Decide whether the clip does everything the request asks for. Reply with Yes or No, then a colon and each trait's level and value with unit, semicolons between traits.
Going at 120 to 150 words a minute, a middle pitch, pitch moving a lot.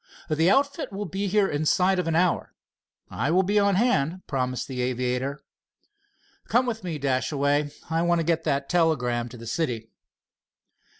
No: average, 165 wpm; medium, 160 Hz; wide, 6.0 semitones